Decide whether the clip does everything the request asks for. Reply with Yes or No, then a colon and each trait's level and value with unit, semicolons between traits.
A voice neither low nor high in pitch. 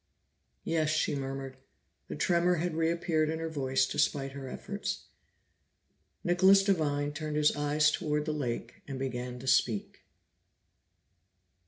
Yes: medium, 150 Hz